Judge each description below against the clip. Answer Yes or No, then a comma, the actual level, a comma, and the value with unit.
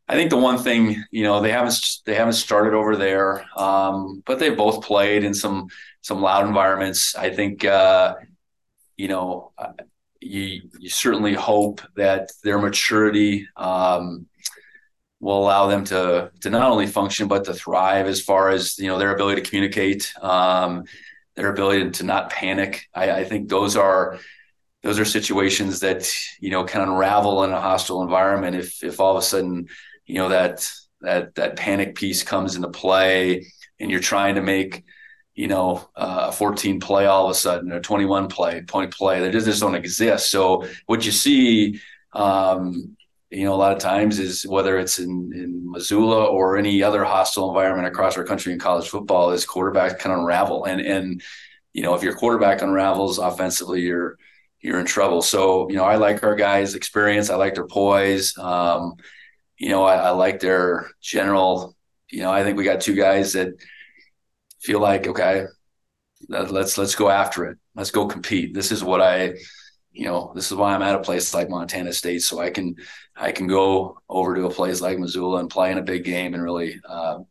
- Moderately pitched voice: No, very low, 95 Hz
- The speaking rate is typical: Yes, average, 190 wpm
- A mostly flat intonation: Yes, narrow, 1.6 semitones